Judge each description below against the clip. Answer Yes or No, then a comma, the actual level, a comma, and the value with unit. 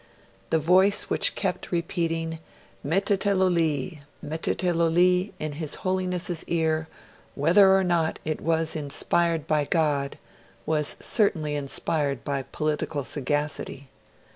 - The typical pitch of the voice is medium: Yes, medium, 160 Hz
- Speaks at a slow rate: Yes, slow, 115 wpm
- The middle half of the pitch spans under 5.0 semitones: Yes, average, 3.1 semitones